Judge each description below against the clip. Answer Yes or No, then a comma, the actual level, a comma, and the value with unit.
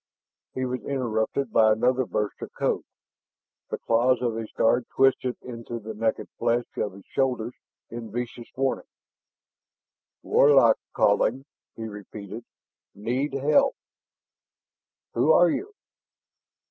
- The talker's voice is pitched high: No, low, 120 Hz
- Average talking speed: No, slow, 125 wpm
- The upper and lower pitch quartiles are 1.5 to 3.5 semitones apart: Yes, average, 2.8 semitones